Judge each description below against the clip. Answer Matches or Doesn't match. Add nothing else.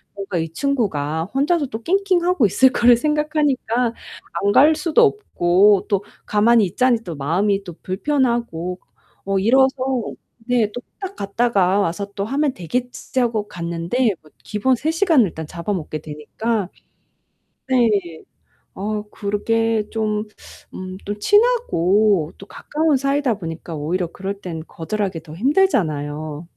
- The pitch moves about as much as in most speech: Doesn't match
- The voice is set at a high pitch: Matches